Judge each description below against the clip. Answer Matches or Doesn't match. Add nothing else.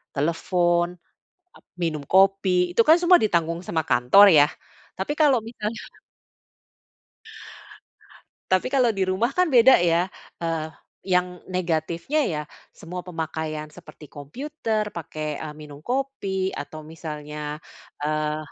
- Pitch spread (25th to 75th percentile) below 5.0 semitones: Doesn't match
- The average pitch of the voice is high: Doesn't match